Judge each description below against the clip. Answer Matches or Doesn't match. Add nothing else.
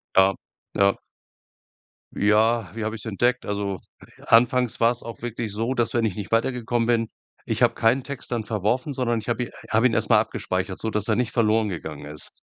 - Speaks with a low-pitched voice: Matches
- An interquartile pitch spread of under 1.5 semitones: Doesn't match